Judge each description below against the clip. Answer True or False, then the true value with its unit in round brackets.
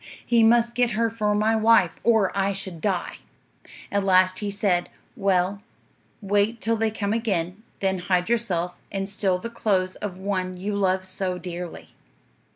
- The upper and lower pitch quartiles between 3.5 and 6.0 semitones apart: False (2.9 semitones)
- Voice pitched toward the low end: False (200 Hz)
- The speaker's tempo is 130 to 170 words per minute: True (165 wpm)